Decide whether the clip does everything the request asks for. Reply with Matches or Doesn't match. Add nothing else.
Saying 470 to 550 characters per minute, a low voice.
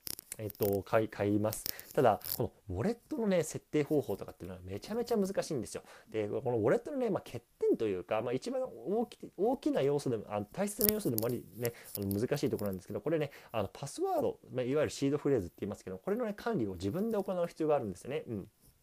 Doesn't match